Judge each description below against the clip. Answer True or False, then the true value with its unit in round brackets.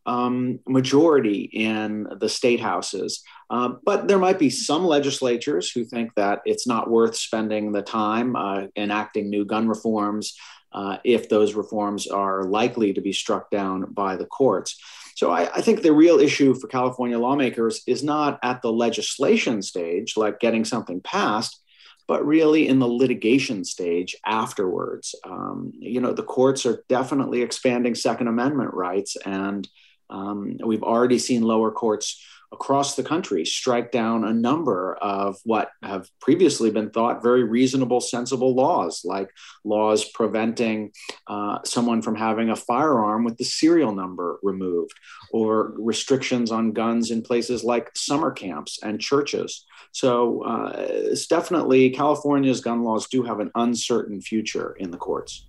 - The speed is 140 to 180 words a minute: True (150 wpm)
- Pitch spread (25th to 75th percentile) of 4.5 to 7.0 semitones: False (2.9 semitones)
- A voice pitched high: False (115 Hz)